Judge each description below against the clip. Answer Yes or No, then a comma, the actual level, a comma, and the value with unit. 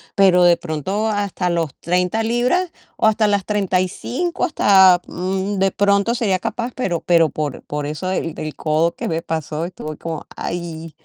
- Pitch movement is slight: No, average, 3.8 semitones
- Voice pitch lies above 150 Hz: Yes, medium, 185 Hz